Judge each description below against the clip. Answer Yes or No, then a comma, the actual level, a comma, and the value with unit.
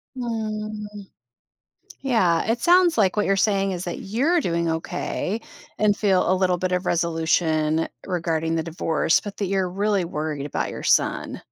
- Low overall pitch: No, medium, 185 Hz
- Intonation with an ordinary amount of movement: Yes, average, 4.4 semitones